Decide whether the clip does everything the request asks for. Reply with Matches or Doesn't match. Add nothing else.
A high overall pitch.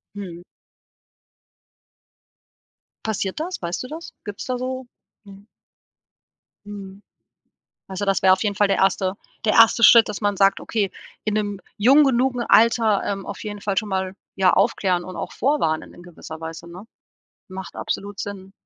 Matches